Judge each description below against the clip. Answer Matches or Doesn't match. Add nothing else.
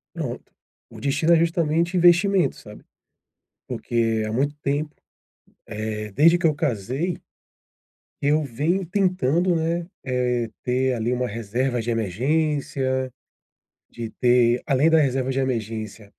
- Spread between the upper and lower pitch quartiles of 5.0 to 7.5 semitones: Matches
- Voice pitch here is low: Matches